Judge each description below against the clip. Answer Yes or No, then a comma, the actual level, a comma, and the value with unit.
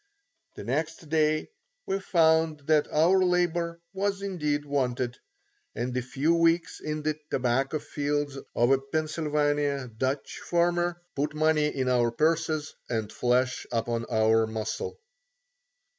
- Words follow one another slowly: Yes, slow, 130 wpm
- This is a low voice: No, medium, 150 Hz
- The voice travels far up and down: No, average, 4.1 semitones